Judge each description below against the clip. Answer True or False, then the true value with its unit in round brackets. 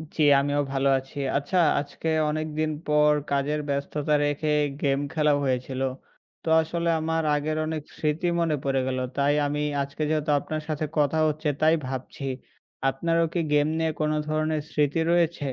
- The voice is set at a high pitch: False (150 Hz)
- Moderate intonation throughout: False (1.7 semitones)